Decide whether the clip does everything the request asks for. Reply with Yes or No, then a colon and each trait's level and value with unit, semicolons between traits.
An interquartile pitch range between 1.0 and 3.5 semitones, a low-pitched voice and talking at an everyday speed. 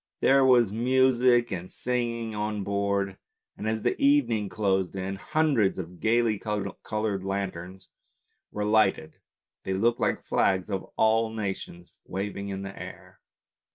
Yes: average, 3.2 semitones; low, 105 Hz; average, 150 wpm